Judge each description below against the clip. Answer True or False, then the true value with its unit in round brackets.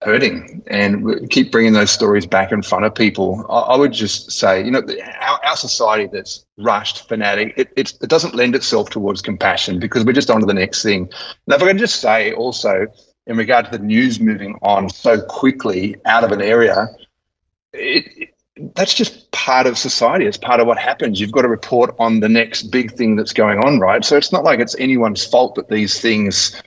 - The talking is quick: True (215 wpm)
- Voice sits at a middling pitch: False (115 Hz)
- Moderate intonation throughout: False (6.0 semitones)